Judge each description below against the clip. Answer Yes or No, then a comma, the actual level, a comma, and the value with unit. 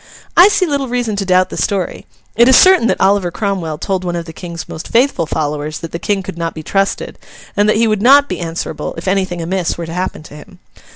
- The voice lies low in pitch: No, high, 190 Hz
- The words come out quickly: Yes, fast, 240 wpm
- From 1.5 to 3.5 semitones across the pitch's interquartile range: No, average, 4.3 semitones